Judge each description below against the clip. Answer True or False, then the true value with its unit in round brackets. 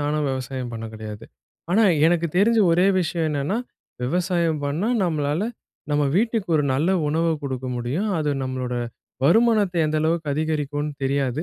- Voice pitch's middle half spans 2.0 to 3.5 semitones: False (4.2 semitones)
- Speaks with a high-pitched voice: False (150 Hz)